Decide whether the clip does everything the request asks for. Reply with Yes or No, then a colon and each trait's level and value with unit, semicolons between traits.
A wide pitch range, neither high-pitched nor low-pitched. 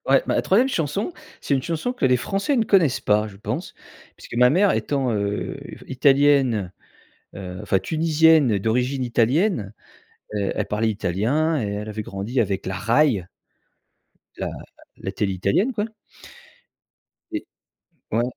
No: wide, 7.3 semitones; low, 125 Hz